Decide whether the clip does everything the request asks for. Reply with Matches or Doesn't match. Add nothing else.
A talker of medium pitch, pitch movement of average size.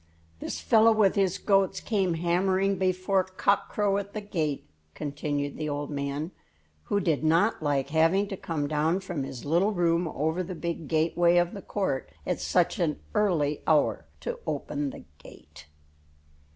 Matches